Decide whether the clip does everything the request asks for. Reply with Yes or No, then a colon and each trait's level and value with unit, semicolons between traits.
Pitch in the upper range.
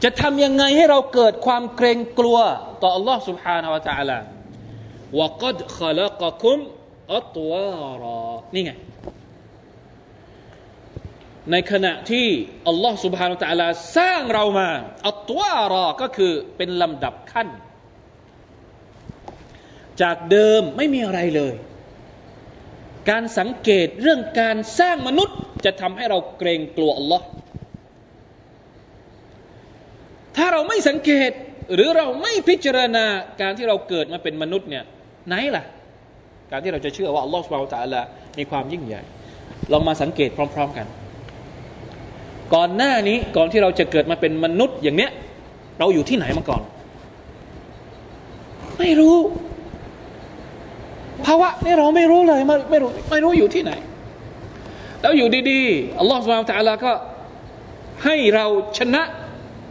Yes: high, 195 Hz